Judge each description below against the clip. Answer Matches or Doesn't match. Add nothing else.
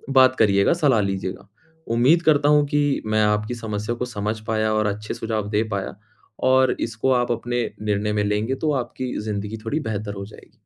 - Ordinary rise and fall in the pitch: Matches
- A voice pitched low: Matches